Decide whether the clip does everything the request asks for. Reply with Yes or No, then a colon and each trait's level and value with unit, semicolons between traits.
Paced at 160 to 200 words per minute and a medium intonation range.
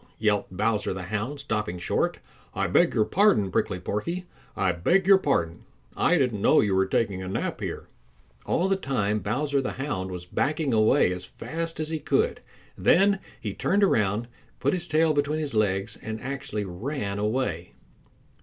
No: average, 175 wpm; wide, 7.6 semitones